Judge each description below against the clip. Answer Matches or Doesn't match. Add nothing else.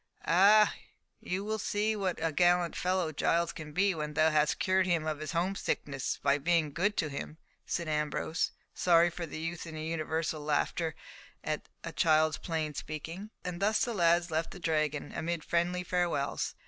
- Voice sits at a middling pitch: Matches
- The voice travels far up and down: Doesn't match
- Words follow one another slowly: Doesn't match